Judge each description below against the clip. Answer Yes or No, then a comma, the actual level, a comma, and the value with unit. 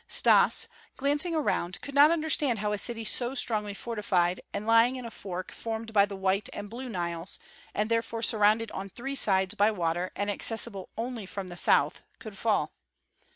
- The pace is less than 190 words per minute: Yes, average, 180 wpm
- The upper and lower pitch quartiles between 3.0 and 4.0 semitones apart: Yes, average, 3.5 semitones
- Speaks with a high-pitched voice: Yes, high, 215 Hz